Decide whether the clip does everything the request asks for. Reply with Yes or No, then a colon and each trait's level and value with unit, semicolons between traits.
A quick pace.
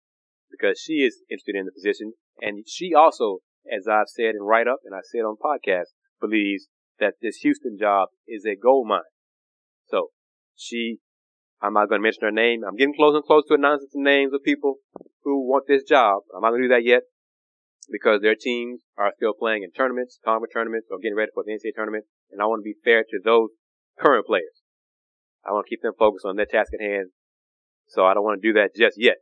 Yes: fast, 220 wpm